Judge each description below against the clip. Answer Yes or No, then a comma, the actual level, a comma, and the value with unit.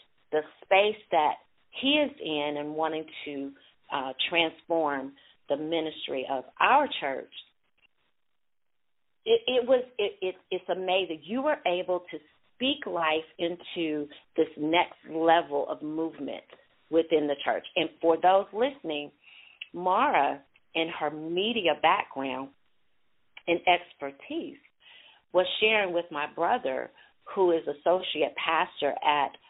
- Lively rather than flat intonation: No, average, 3.8 semitones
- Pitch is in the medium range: Yes, medium, 165 Hz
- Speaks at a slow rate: Yes, slow, 115 wpm